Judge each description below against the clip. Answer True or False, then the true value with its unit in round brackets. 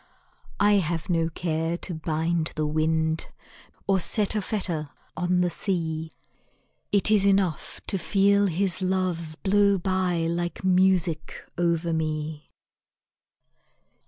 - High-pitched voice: False (175 Hz)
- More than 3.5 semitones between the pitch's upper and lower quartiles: False (3.0 semitones)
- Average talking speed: False (120 wpm)